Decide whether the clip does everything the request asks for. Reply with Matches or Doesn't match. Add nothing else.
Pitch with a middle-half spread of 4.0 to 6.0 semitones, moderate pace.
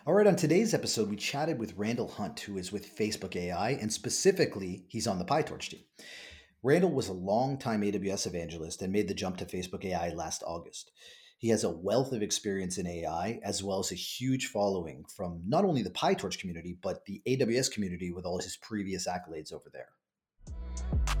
Doesn't match